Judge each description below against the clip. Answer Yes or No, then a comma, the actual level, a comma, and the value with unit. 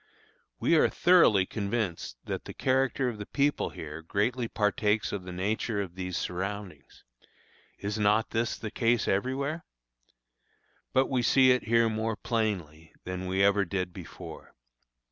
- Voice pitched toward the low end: Yes, low, 105 Hz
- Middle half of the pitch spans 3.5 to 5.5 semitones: Yes, average, 4.2 semitones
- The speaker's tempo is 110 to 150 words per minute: Yes, average, 145 wpm